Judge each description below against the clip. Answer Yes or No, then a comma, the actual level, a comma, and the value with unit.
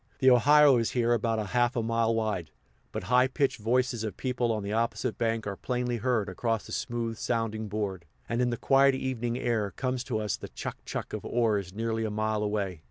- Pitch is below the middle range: Yes, low, 115 Hz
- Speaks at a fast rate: Yes, fast, 210 wpm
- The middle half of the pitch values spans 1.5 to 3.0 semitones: Yes, narrow, 2.4 semitones